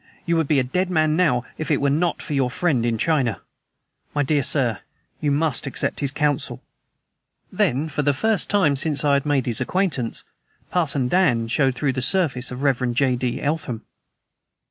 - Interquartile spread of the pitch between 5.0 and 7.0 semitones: No, average, 3.7 semitones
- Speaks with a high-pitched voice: No, medium, 140 Hz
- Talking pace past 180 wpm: Yes, average, 190 wpm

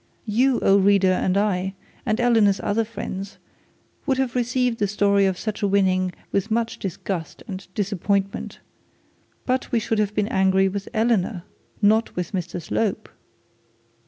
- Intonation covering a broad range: No, average, 2.9 semitones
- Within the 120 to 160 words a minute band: Yes, average, 150 wpm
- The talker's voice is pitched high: Yes, high, 200 Hz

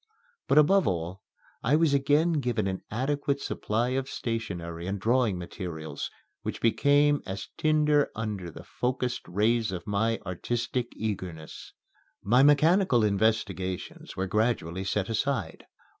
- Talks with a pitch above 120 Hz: No, low, 115 Hz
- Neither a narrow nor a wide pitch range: No, wide, 6.4 semitones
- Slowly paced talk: Yes, slow, 130 wpm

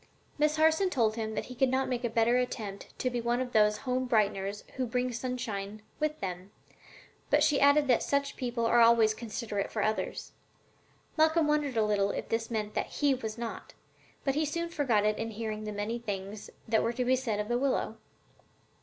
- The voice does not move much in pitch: No, average, 3.4 semitones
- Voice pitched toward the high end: Yes, high, 235 Hz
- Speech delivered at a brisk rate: Yes, fast, 210 wpm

